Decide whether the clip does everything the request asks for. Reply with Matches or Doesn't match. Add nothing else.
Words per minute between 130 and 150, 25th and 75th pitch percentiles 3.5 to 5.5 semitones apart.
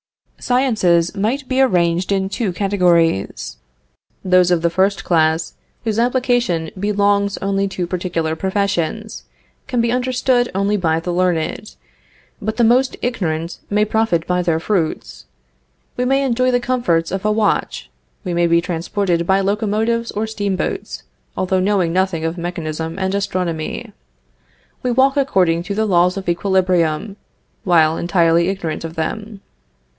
Matches